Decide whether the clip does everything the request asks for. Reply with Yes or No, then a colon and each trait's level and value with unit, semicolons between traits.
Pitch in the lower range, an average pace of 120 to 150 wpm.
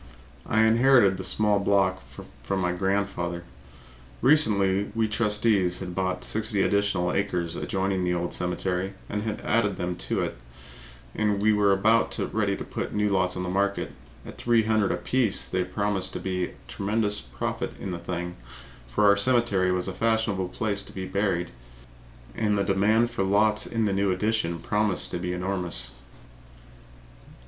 No: low, 100 Hz; average, 175 wpm